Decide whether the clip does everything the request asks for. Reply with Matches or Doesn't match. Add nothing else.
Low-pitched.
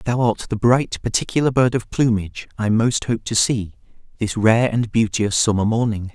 Matches